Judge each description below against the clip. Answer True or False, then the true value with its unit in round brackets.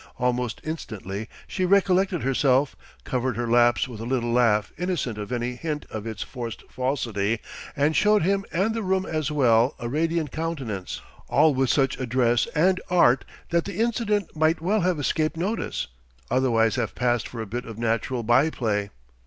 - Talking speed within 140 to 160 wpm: False (170 wpm)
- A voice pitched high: False (130 Hz)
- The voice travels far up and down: True (5.9 semitones)